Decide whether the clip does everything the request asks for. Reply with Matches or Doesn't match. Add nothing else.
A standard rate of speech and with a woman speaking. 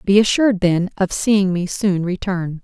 Matches